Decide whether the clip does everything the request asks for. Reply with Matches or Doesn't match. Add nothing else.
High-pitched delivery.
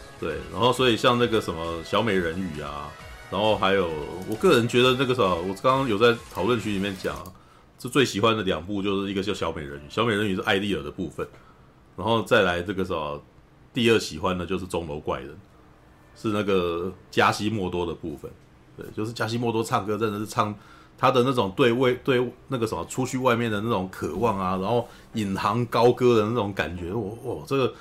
Doesn't match